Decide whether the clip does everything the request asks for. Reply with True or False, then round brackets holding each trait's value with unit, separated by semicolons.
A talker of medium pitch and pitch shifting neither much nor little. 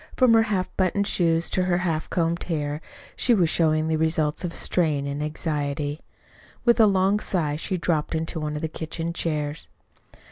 True (165 Hz; 3.2 semitones)